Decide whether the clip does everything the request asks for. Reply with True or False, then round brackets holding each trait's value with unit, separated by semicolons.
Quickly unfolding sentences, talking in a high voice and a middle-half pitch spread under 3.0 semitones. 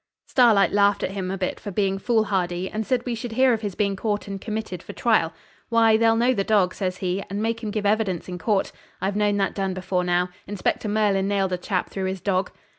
True (235 wpm; 200 Hz; 2.6 semitones)